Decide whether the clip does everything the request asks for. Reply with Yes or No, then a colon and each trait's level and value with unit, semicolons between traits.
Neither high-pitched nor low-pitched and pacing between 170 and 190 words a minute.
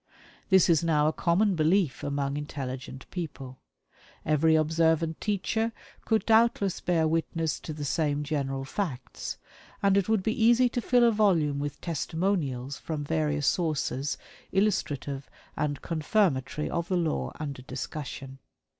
No: medium, 160 Hz; slow, 135 wpm